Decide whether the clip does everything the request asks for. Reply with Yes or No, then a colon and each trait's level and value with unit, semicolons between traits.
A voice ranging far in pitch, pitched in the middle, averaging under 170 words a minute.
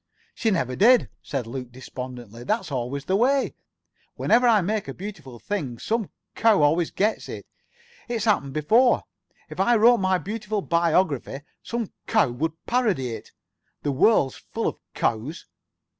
Yes: wide, 8.6 semitones; medium, 175 Hz; average, 150 wpm